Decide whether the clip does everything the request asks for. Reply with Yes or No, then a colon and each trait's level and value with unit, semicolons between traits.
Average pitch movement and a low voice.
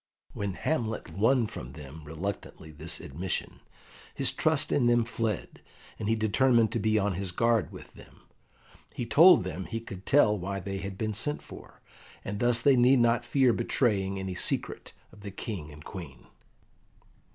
Yes: average, 4.2 semitones; low, 105 Hz